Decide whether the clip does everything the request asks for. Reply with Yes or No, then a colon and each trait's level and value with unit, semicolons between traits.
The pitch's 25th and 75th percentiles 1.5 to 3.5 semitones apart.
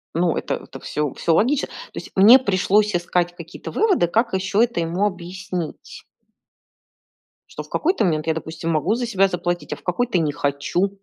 No: average, 4.0 semitones